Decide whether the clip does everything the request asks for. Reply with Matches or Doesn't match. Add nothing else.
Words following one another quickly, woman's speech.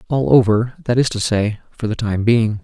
Doesn't match